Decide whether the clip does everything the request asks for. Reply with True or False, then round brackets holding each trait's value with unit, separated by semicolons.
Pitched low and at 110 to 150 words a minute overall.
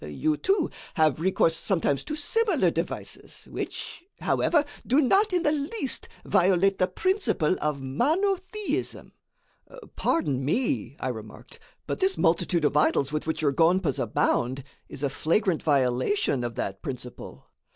False (165 Hz; 140 wpm)